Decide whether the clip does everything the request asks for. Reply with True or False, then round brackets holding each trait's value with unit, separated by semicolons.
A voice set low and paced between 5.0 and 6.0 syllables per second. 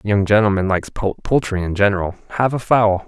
True (105 Hz; 5.5 syllables/s)